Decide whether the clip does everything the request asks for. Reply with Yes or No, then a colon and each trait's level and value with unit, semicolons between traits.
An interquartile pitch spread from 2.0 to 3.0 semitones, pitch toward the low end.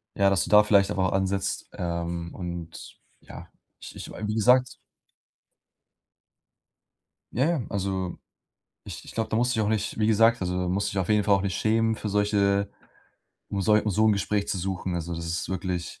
Yes: average, 2.7 semitones; low, 100 Hz